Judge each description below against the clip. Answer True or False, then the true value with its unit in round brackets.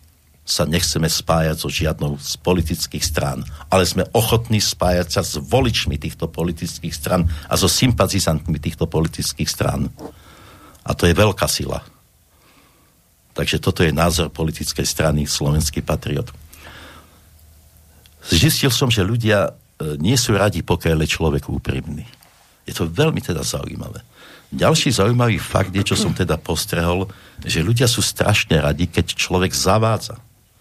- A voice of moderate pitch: False (85 Hz)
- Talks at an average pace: True (135 wpm)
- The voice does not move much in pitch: False (4.0 semitones)